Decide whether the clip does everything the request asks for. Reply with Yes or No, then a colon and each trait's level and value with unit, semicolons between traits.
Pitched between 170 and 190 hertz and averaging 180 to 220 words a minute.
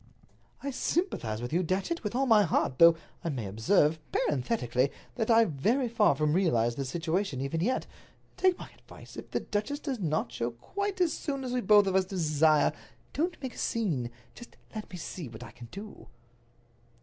Yes: medium, 185 Hz; average, 190 wpm